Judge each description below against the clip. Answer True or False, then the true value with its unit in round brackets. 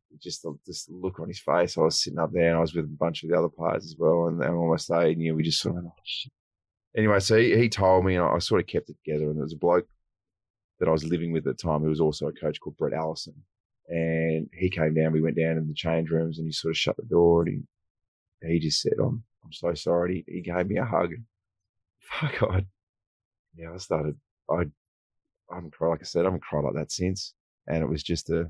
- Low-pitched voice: True (85 Hz)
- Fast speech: True (270 wpm)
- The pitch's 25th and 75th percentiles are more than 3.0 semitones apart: False (2.7 semitones)